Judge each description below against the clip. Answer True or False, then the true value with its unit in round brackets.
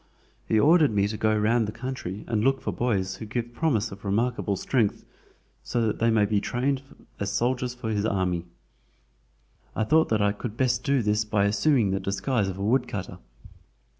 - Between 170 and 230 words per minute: True (190 wpm)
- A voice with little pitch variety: False (3.4 semitones)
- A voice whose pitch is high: False (110 Hz)